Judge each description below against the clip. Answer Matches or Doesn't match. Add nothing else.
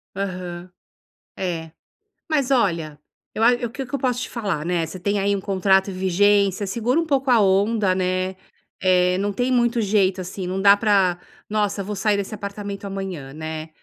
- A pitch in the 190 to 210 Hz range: Matches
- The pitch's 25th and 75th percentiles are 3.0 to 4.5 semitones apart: Doesn't match